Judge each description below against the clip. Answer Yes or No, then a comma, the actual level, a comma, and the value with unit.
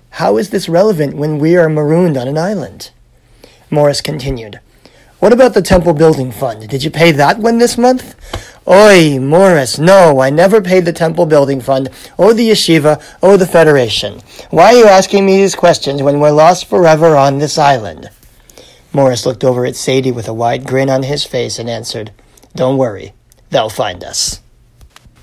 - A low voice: No, medium, 150 Hz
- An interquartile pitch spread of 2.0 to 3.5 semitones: No, average, 5.0 semitones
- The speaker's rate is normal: Yes, average, 180 wpm